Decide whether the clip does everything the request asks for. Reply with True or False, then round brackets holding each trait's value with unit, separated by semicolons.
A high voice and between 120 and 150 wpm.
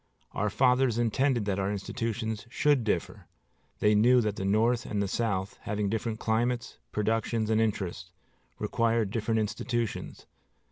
False (110 Hz; 140 wpm)